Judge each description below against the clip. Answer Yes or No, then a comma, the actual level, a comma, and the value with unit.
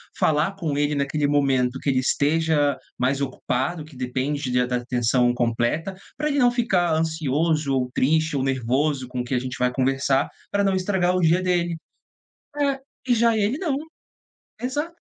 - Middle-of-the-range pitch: Yes, medium, 145 Hz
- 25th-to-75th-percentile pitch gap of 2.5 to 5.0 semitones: No, wide, 5.6 semitones